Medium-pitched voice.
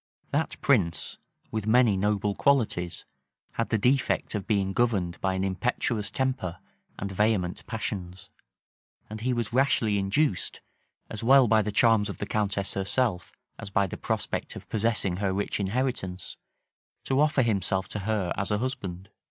No: low, 105 Hz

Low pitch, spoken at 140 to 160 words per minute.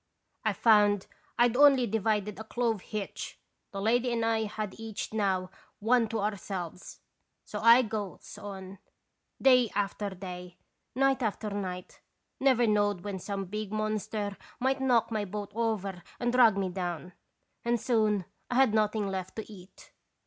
No: high, 210 Hz; average, 150 wpm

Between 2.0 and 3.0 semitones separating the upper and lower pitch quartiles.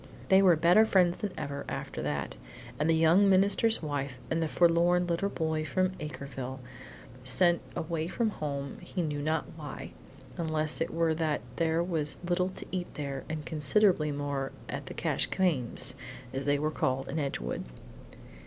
No: average, 3.6 semitones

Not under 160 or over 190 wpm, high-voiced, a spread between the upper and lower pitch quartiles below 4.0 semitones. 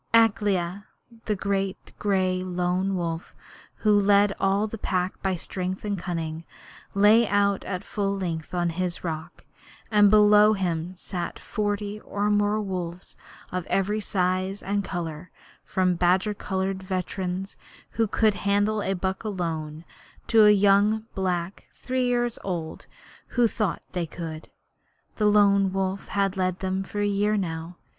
No: average, 140 wpm; high, 195 Hz; narrow, 2.4 semitones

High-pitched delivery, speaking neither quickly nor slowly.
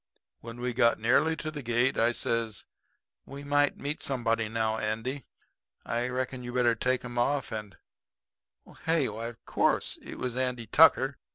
No: low, 120 Hz; average, 170 wpm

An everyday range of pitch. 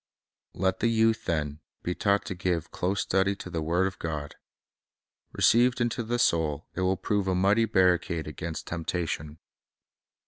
Yes: average, 3.4 semitones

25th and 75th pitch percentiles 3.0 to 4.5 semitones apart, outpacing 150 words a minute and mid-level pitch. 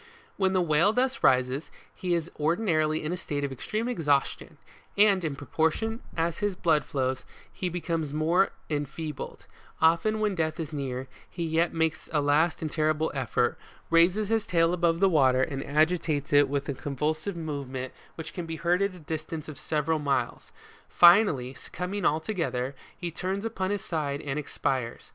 Yes: average, 3.8 semitones; average, 170 wpm; medium, 160 Hz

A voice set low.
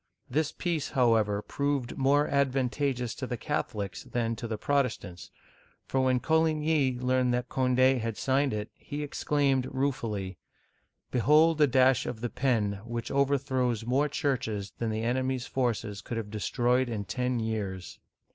Yes: low, 125 Hz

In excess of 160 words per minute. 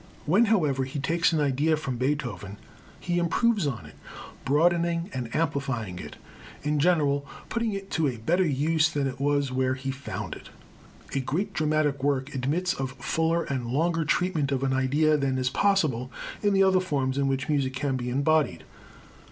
Yes: average, 175 wpm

